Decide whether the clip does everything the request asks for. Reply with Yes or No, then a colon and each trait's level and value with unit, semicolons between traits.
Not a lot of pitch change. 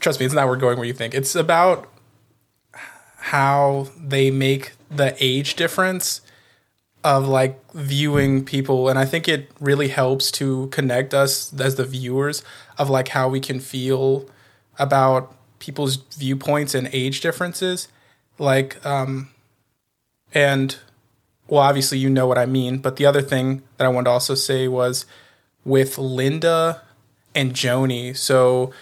Yes: narrow, 1.5 semitones